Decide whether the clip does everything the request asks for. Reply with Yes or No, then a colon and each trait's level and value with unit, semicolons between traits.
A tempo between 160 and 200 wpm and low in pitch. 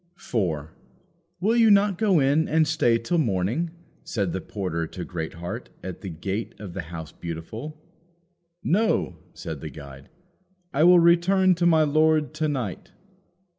No: average, 150 wpm; low, 125 Hz